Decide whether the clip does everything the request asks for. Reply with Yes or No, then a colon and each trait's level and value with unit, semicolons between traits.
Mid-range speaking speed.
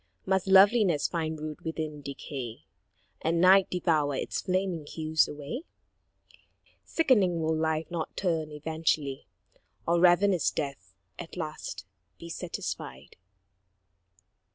No: slow, 105 wpm